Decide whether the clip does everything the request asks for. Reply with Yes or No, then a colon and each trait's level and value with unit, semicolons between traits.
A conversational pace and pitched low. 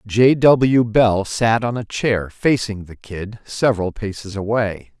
Yes: average, 155 wpm; low, 110 Hz